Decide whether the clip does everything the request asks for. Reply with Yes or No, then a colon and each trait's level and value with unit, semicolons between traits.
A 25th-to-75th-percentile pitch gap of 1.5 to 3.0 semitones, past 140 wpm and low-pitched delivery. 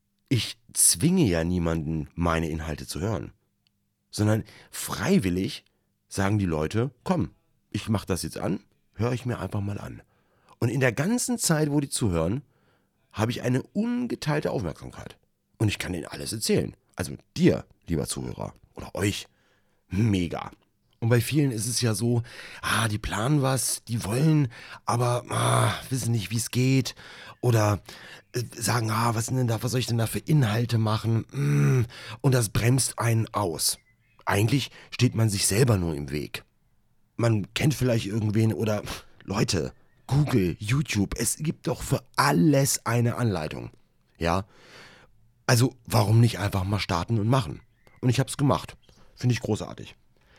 No: average, 3.8 semitones; average, 155 wpm; low, 115 Hz